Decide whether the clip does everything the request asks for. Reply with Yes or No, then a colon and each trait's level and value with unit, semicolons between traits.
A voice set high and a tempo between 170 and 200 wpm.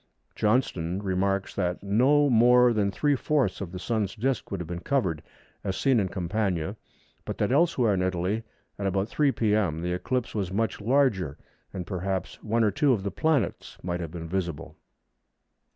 No: low, 100 Hz; average, 175 wpm